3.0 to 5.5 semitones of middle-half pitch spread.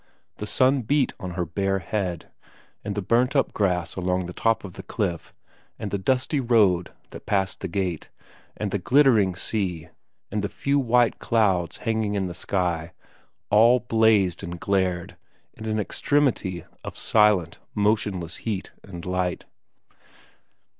Yes: average, 3.8 semitones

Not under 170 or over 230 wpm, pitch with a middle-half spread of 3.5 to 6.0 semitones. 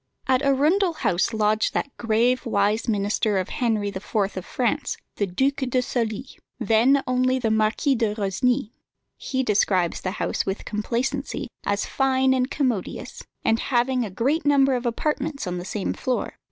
No: average, 160 wpm; average, 4.0 semitones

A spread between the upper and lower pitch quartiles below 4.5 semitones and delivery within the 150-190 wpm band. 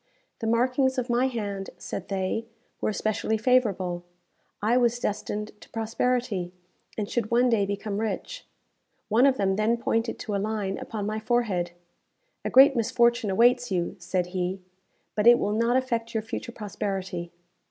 Yes: average, 3.3 semitones; average, 160 wpm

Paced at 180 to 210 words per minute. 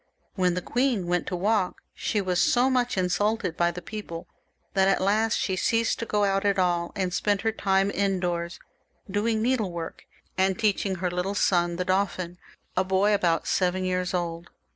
Yes: average, 185 wpm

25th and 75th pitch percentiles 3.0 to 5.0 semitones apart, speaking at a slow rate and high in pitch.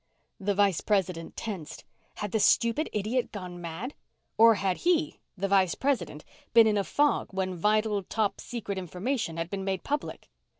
No: average, 3.7 semitones; average, 165 wpm; high, 200 Hz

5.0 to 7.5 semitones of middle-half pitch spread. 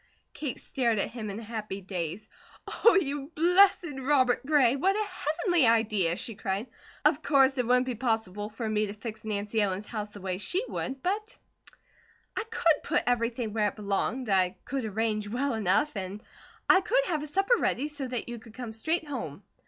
Yes: wide, 5.6 semitones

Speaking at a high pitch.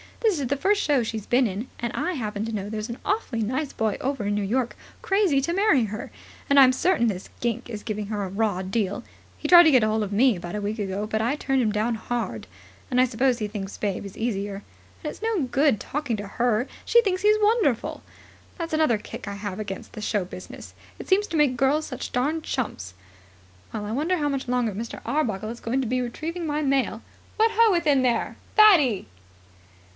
Yes: high, 240 Hz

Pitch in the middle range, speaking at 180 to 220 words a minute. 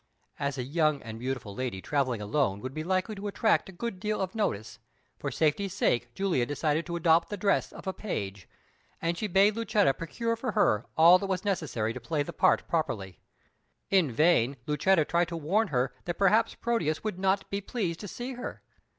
Yes: medium, 170 Hz; average, 200 wpm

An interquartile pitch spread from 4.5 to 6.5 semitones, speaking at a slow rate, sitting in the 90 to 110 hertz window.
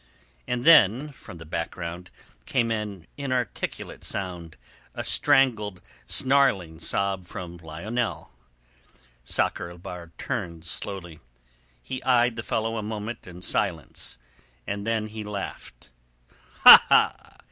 Yes: average, 5.0 semitones; slow, 110 wpm; low, 100 Hz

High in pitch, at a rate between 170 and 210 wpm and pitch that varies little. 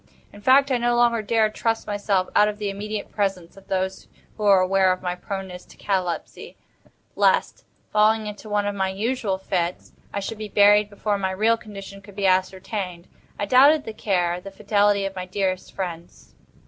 Yes: high, 200 Hz; average, 185 wpm; narrow, 2.1 semitones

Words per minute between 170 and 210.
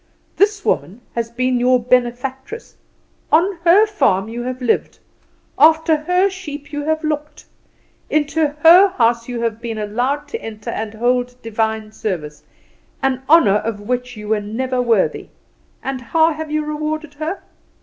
No: average, 150 wpm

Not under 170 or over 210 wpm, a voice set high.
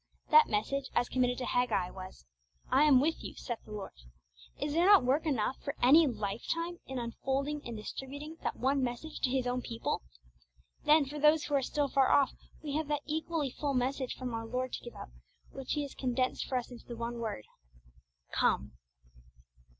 Yes: average, 195 wpm; very high, 265 Hz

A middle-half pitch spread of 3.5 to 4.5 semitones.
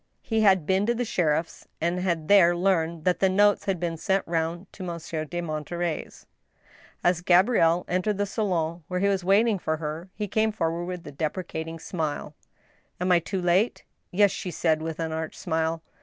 No: average, 2.8 semitones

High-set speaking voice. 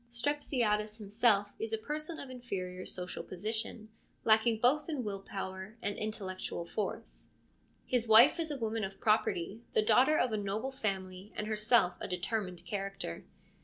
Yes: high, 215 Hz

